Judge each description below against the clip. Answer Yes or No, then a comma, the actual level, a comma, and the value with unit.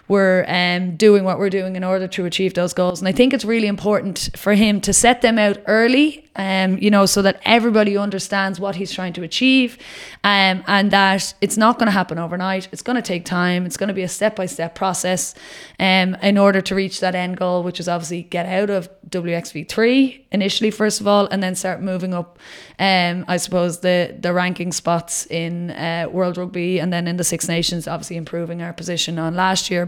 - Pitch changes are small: Yes, narrow, 2.3 semitones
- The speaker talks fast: Yes, fast, 220 wpm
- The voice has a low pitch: No, medium, 185 Hz